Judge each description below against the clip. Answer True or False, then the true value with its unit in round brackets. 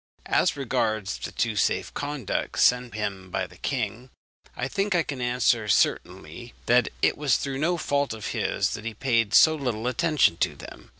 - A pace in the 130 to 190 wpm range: True (180 wpm)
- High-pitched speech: False (125 Hz)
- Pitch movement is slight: False (4.6 semitones)